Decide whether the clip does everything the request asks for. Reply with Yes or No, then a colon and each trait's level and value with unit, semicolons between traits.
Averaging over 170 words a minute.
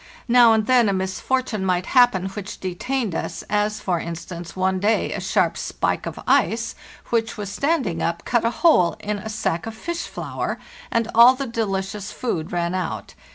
Yes: average, 180 wpm